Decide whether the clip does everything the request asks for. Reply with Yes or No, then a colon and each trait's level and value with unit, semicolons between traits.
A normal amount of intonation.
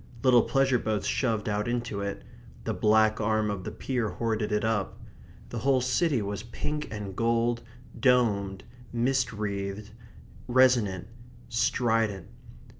Yes: average, 3.0 semitones